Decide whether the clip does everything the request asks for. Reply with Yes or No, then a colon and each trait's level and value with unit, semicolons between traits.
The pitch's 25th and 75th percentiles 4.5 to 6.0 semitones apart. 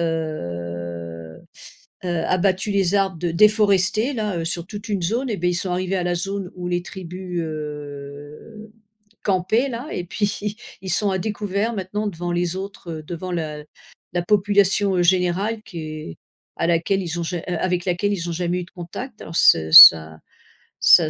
No: average, 3.3 semitones